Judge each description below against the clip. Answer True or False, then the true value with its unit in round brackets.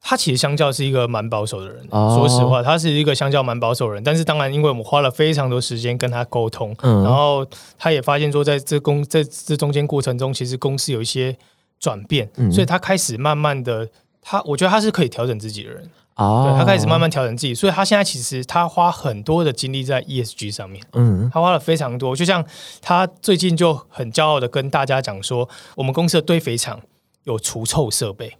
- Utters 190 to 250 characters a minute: False (335 characters per minute)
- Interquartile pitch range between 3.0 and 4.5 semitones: True (4.2 semitones)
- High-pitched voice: False (135 Hz)